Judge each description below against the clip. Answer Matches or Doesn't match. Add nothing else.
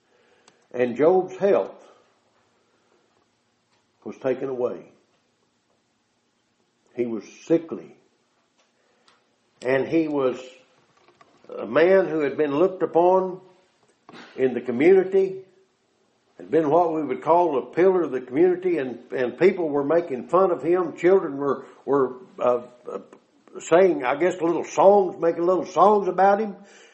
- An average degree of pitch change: Doesn't match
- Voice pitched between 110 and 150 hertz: Doesn't match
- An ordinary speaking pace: Doesn't match